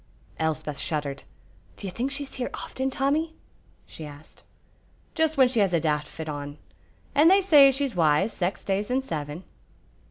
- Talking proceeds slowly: No, average, 165 wpm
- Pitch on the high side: Yes, high, 195 Hz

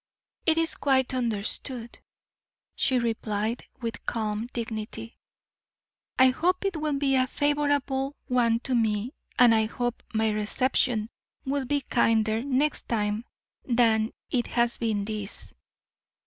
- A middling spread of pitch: Yes, average, 3.3 semitones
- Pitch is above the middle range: Yes, high, 240 Hz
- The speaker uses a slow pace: Yes, slow, 125 wpm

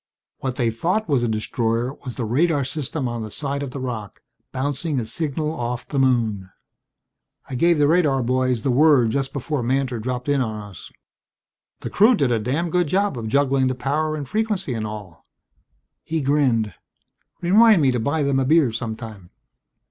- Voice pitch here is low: Yes, low, 130 Hz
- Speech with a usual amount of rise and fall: Yes, average, 4.2 semitones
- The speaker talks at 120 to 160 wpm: No, average, 185 wpm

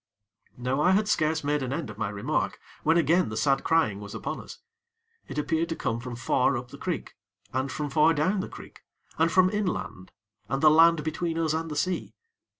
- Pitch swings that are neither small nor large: Yes, average, 4.1 semitones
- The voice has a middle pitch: Yes, medium, 155 Hz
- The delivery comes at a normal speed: No, fast, 210 wpm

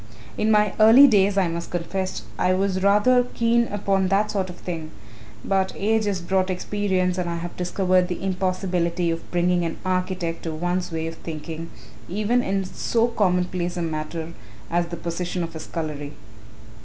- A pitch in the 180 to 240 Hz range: Yes, medium, 185 Hz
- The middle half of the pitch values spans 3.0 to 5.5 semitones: No, narrow, 2.6 semitones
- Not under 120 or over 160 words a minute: No, average, 170 wpm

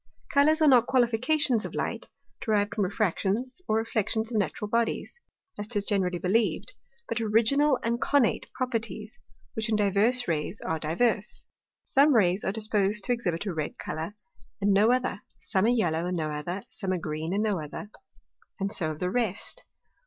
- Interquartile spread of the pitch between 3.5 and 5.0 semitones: Yes, average, 4.1 semitones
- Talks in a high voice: Yes, high, 210 Hz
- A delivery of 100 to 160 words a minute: No, average, 175 wpm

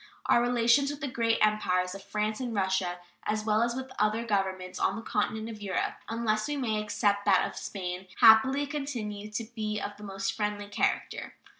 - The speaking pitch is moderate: No, high, 215 Hz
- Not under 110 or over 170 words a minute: No, average, 195 wpm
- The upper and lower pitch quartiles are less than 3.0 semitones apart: Yes, narrow, 2.5 semitones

